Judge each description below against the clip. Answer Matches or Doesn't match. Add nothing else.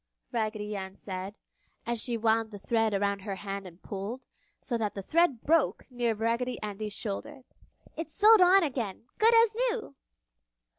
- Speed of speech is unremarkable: Matches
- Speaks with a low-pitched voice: Doesn't match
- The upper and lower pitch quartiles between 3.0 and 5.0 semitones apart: Doesn't match